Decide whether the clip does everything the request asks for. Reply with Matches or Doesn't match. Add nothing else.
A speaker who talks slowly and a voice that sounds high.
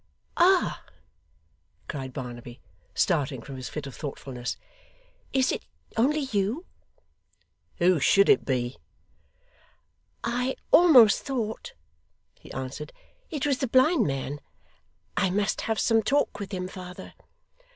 Matches